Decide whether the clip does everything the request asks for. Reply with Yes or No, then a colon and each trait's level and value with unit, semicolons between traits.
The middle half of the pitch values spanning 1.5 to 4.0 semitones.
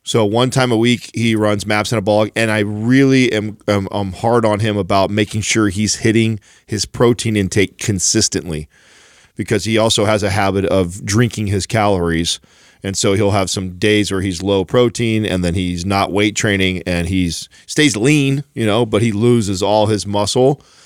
Yes: narrow, 2.5 semitones